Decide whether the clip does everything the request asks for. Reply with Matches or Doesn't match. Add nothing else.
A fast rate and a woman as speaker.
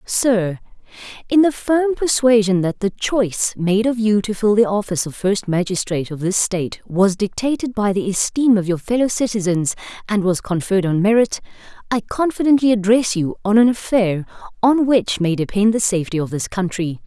Doesn't match